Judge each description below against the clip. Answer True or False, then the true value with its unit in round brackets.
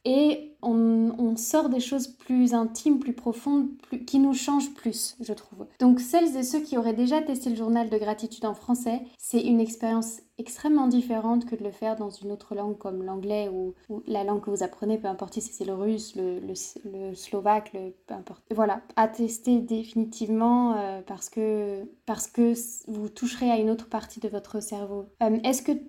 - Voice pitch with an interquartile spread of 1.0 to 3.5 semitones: True (2.8 semitones)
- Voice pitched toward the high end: True (225 Hz)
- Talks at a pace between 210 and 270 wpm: False (200 wpm)